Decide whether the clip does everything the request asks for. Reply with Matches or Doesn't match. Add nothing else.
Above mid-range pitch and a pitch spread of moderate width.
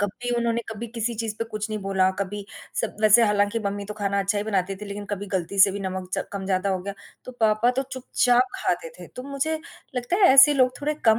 Matches